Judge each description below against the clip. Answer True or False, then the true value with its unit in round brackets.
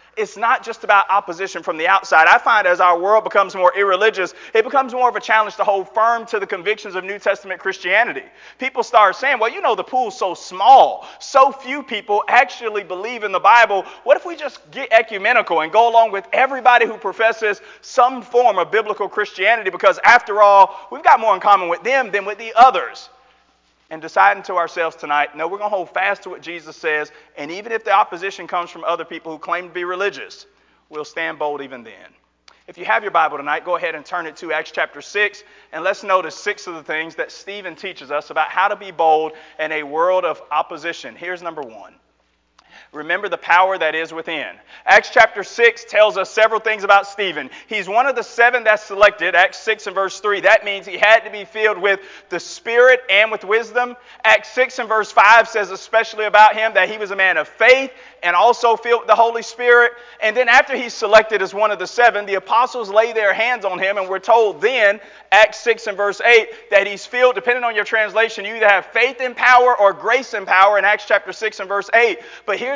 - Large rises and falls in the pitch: False (3.6 semitones)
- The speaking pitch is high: True (210 Hz)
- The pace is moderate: False (225 wpm)